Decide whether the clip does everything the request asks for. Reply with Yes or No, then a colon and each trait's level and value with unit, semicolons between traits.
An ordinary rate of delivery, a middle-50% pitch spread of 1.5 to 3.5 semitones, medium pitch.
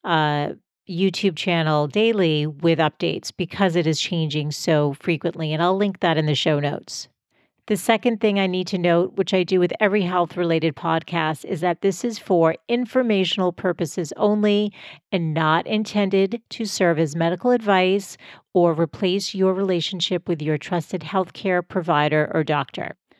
Yes: average, 160 wpm; average, 3.1 semitones; medium, 180 Hz